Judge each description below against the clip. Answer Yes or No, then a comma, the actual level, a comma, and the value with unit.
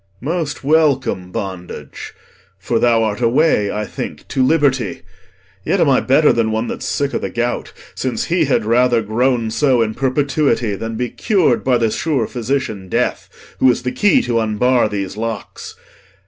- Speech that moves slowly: No, average, 175 wpm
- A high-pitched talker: No, low, 120 Hz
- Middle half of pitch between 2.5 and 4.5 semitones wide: Yes, average, 3.7 semitones